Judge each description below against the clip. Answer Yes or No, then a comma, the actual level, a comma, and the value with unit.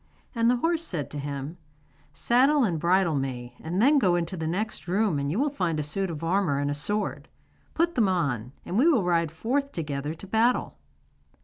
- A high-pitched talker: No, medium, 175 Hz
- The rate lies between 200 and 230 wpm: Yes, fast, 205 wpm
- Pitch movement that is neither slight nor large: No, wide, 7.5 semitones